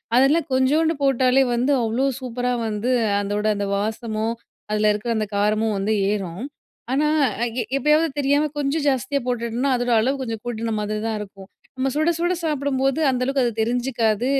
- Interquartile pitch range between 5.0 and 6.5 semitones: No, average, 4.0 semitones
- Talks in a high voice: Yes, high, 245 Hz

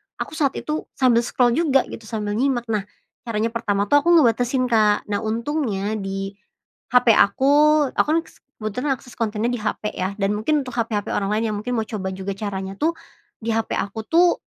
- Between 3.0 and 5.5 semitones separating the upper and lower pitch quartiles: Yes, average, 4.0 semitones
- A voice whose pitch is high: Yes, high, 230 Hz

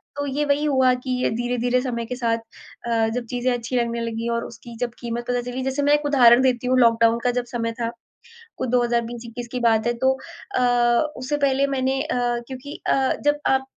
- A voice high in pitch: Yes, high, 245 Hz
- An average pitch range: No, narrow, 1.9 semitones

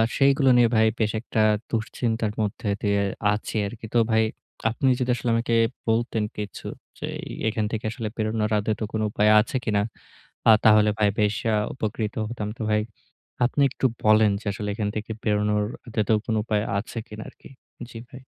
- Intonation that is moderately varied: No, narrow, 1.5 semitones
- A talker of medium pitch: No, low, 110 Hz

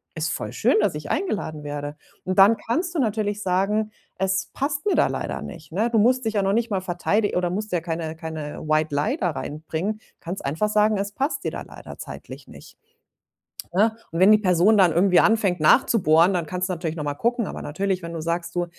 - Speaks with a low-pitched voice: No, medium, 185 Hz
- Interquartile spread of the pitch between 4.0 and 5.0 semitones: Yes, average, 4.7 semitones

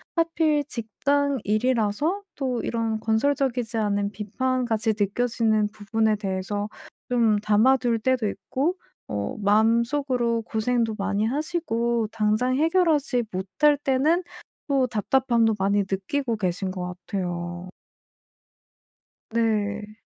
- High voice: Yes, high, 225 Hz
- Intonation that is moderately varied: Yes, average, 3.9 semitones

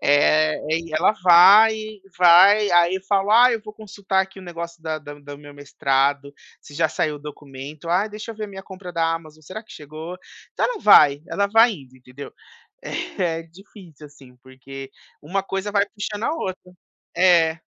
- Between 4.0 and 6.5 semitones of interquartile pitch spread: Yes, average, 5.2 semitones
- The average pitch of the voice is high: No, medium, 170 Hz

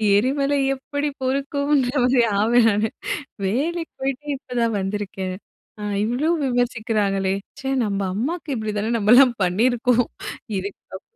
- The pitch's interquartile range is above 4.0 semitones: Yes, average, 4.5 semitones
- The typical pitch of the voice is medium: No, high, 245 Hz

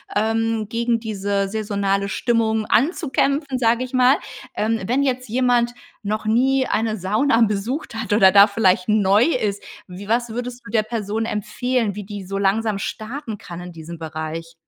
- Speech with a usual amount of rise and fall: Yes, average, 3.2 semitones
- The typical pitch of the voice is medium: No, high, 220 Hz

